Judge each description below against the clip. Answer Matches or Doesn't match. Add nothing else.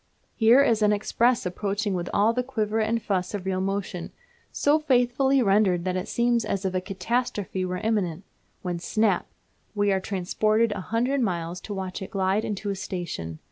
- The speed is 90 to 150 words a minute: Doesn't match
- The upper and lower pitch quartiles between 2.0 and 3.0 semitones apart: Doesn't match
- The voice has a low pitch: Doesn't match